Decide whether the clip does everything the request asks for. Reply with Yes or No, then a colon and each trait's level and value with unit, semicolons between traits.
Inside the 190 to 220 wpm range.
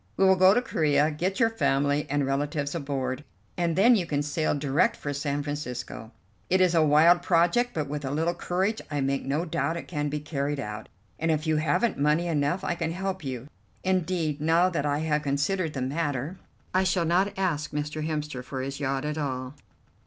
Yes: fast, 205 wpm